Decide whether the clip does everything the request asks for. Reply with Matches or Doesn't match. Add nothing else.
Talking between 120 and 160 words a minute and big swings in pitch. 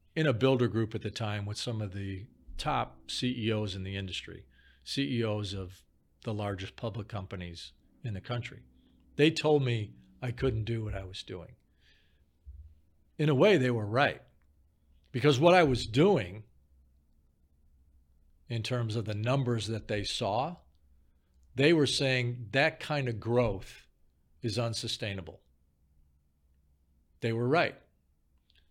Matches